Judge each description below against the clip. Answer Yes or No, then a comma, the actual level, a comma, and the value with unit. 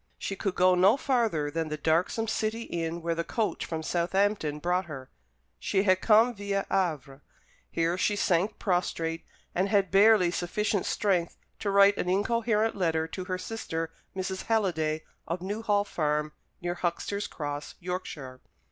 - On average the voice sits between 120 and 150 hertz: No, medium, 185 Hz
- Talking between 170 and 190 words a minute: No, average, 155 wpm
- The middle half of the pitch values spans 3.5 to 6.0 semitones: Yes, average, 3.8 semitones